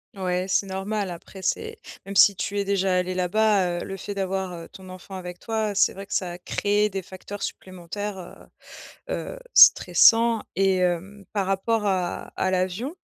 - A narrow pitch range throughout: Yes, narrow, 1.9 semitones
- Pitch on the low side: No, high, 195 Hz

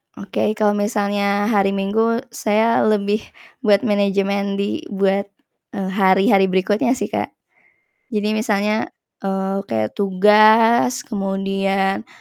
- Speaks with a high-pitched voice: Yes, high, 200 Hz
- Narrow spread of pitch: Yes, narrow, 1.6 semitones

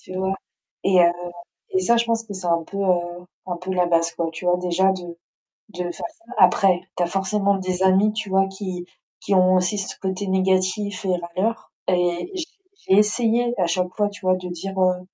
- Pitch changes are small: Yes, narrow, 2.0 semitones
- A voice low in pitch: No, medium, 185 Hz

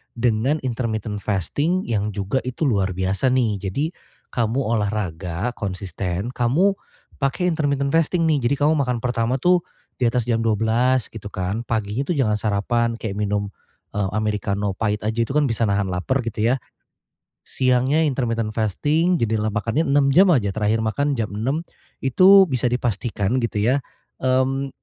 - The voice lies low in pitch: Yes, low, 115 Hz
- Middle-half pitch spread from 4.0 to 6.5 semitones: Yes, average, 4.5 semitones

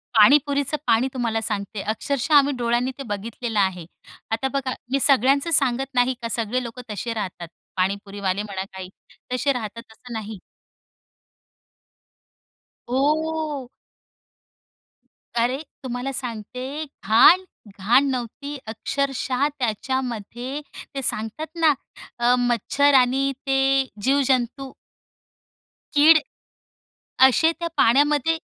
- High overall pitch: Yes, very high, 250 Hz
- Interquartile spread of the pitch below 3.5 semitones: No, average, 3.8 semitones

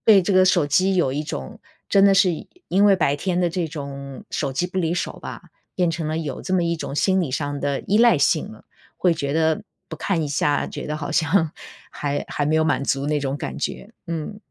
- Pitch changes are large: No, average, 4.2 semitones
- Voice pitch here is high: No, medium, 160 Hz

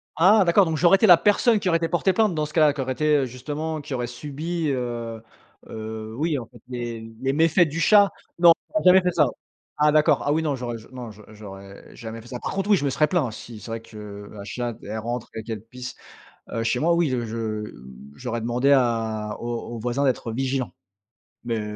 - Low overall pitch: Yes, low, 125 Hz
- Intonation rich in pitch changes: Yes, wide, 5.8 semitones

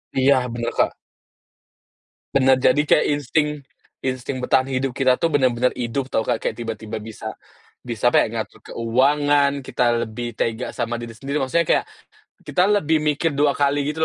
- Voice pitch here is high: No, low, 130 Hz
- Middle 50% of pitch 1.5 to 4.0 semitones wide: Yes, average, 3.4 semitones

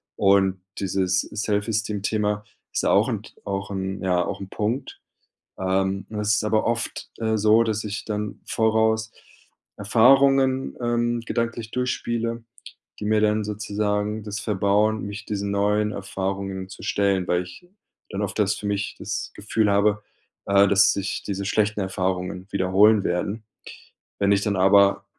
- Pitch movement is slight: Yes, narrow, 1.9 semitones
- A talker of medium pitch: No, low, 105 Hz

